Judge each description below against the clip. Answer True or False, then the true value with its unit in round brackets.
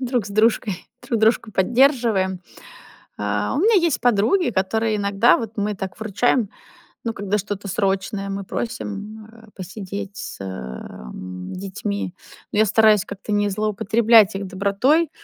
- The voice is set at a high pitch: True (205 Hz)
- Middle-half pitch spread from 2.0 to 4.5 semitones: True (2.7 semitones)